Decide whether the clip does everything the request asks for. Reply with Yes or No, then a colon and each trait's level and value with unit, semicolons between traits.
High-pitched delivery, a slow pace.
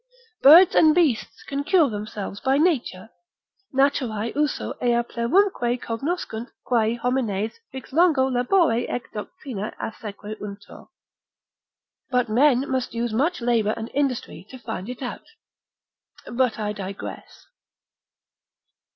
Yes: high, 245 Hz; slow, 115 wpm